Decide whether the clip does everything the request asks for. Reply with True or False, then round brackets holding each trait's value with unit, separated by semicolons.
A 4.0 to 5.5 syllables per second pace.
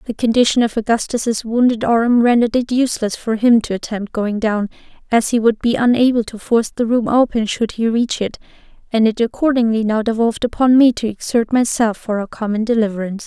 False (5.8 syllables/s)